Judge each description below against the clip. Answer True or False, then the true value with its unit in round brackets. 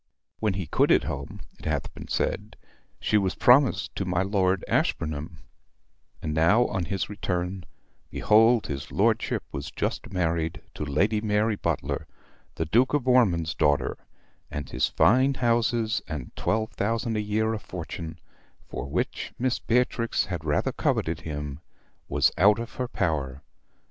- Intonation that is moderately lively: False (5.9 semitones)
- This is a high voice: False (100 Hz)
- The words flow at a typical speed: True (150 wpm)